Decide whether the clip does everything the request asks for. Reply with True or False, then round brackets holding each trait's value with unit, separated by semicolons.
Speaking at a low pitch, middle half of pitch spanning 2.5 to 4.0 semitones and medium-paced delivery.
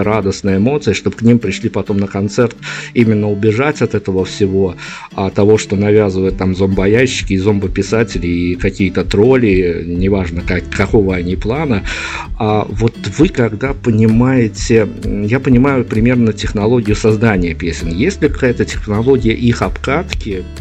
True (105 Hz; 3.1 semitones; 135 wpm)